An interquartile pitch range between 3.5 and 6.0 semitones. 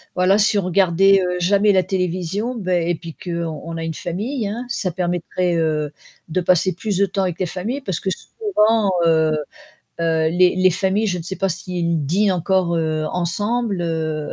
No: average, 2.9 semitones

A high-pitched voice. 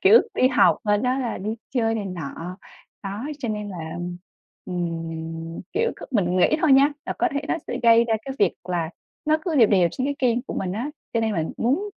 Yes: high, 215 Hz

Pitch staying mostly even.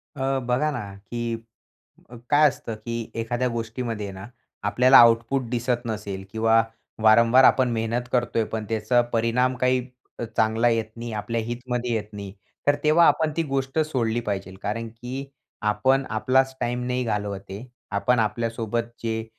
Yes: narrow, 2.2 semitones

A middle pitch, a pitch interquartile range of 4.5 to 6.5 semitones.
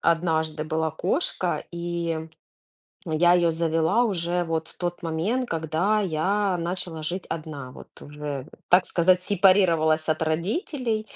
No: medium, 170 Hz; average, 2.7 semitones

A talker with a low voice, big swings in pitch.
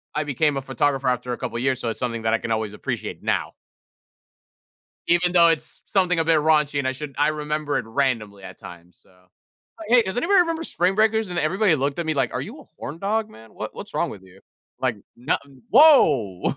No: medium, 145 Hz; wide, 6.7 semitones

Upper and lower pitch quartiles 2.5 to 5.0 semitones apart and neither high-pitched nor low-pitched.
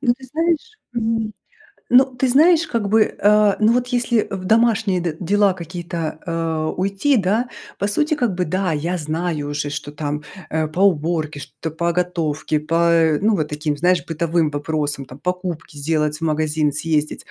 No: wide, 5.6 semitones; medium, 175 Hz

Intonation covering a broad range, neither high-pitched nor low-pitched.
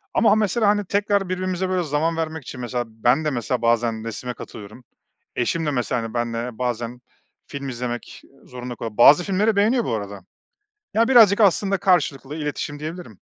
Yes: wide, 7.6 semitones; medium, 145 Hz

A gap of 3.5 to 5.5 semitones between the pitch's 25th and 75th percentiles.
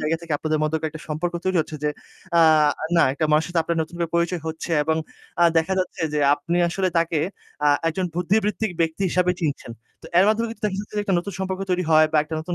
No: average, 2.9 semitones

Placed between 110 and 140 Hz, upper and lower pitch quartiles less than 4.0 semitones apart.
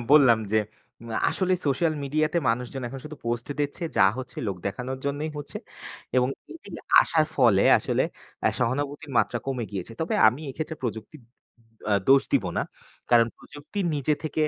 No: low, 135 Hz; average, 4.3 semitones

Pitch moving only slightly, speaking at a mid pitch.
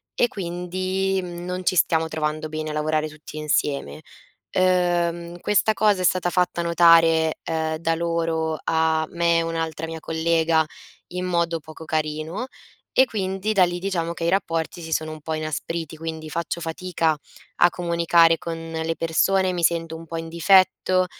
Yes: narrow, 1.8 semitones; medium, 165 Hz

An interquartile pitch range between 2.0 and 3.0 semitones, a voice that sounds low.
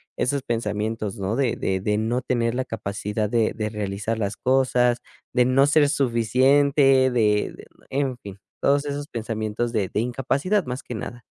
No: average, 3.7 semitones; low, 120 Hz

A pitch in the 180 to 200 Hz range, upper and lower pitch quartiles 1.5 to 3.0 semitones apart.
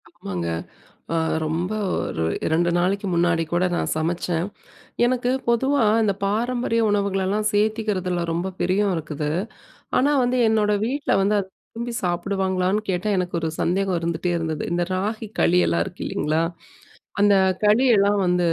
No: high, 190 Hz; average, 3.6 semitones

